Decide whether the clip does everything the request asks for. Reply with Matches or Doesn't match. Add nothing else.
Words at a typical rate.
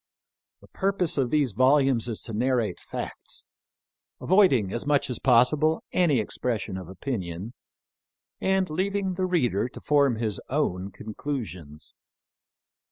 Doesn't match